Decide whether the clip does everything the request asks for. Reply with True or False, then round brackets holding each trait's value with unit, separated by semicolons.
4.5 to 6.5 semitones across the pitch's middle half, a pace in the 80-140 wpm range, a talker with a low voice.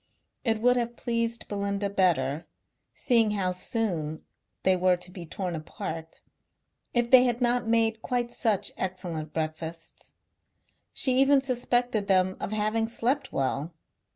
False (5.2 semitones; 135 wpm; 210 Hz)